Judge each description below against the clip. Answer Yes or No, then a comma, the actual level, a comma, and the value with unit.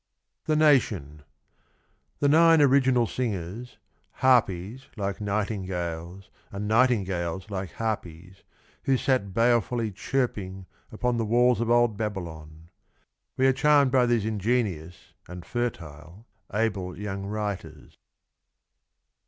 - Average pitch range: Yes, average, 4.9 semitones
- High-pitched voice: No, low, 105 Hz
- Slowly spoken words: Yes, slow, 105 wpm